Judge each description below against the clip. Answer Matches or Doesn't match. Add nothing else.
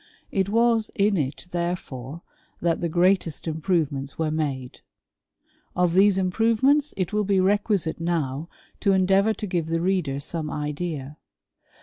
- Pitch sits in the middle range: Matches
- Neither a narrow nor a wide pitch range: Matches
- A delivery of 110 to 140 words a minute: Matches